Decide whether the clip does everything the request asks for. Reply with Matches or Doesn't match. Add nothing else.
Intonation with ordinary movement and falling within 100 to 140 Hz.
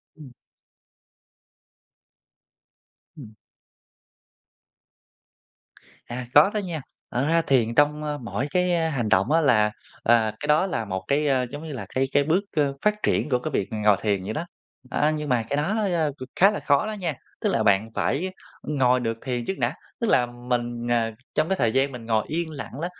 Matches